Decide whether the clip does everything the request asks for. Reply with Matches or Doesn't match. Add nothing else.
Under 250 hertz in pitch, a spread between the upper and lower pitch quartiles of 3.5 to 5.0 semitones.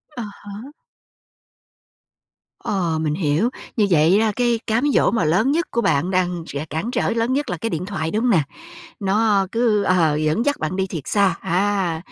Doesn't match